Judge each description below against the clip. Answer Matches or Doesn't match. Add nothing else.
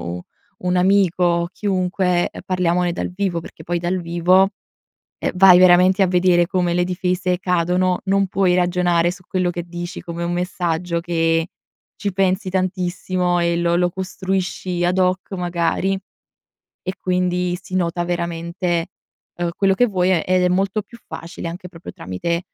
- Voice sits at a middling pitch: Matches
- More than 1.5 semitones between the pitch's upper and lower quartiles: Doesn't match